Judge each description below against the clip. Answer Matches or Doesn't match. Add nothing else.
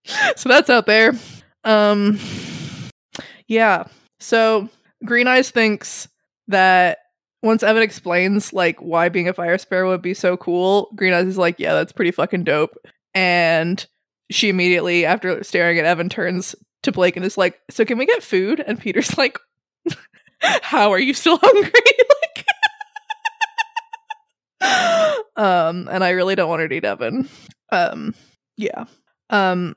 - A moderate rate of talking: Matches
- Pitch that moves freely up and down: Matches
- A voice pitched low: Doesn't match